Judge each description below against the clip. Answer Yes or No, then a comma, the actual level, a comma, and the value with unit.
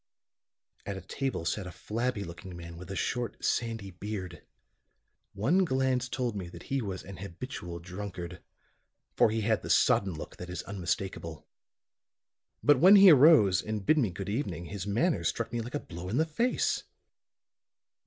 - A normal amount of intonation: No, wide, 5.9 semitones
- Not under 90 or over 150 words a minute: No, average, 170 wpm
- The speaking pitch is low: Yes, low, 100 Hz